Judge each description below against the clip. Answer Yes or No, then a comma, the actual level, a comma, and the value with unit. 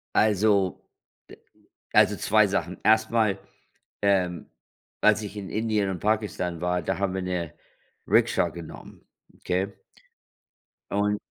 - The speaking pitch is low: Yes, low, 100 Hz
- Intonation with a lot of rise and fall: No, average, 2.7 semitones